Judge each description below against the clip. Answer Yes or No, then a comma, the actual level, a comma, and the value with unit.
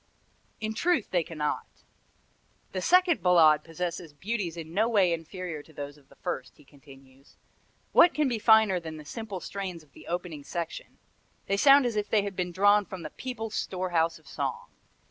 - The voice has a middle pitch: Yes, medium, 180 Hz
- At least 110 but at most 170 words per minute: No, average, 185 wpm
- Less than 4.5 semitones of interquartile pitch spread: No, average, 5.2 semitones